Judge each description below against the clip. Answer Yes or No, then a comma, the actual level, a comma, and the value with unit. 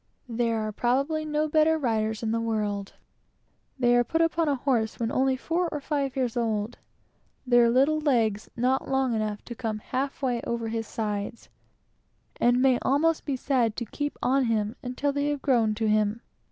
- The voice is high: Yes, high, 245 Hz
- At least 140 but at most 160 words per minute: No, average, 180 wpm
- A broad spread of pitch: No, average, 3.8 semitones